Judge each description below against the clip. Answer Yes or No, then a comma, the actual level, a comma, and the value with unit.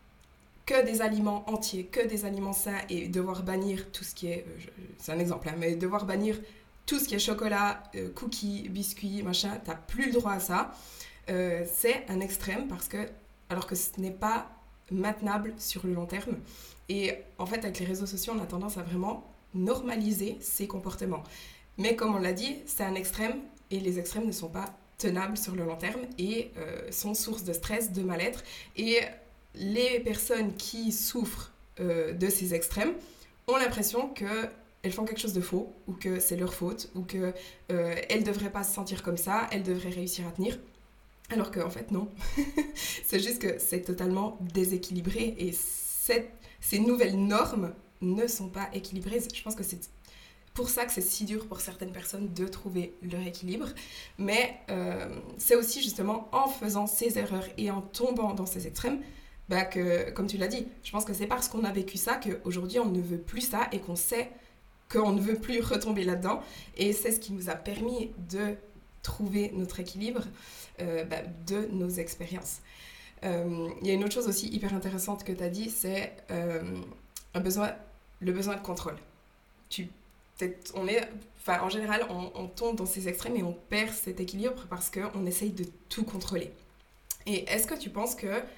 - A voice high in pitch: Yes, high, 200 Hz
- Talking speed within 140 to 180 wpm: No, average, 190 wpm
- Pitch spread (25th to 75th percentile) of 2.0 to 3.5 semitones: Yes, average, 3.2 semitones